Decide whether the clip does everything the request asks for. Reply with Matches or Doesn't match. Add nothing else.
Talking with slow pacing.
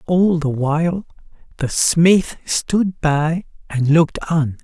Matches